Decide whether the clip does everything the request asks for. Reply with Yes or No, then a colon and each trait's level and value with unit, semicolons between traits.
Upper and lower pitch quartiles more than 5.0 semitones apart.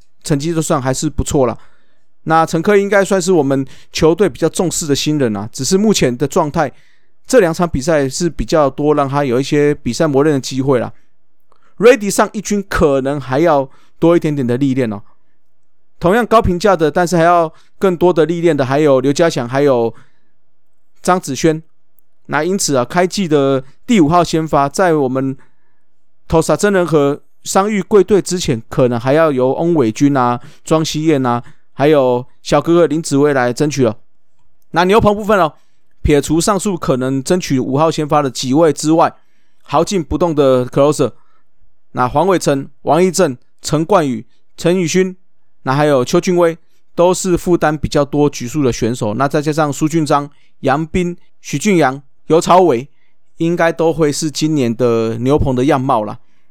No: average, 4.3 semitones